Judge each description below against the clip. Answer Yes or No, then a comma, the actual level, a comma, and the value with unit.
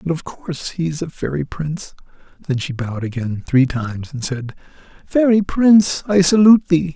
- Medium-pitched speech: Yes, medium, 160 Hz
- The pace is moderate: Yes, average, 180 wpm